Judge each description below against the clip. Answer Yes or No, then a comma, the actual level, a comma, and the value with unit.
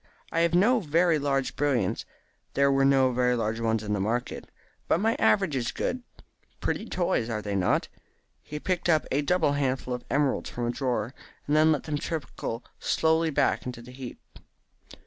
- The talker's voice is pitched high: No, low, 135 Hz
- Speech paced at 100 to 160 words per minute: No, average, 185 wpm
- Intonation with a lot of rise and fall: No, average, 4.9 semitones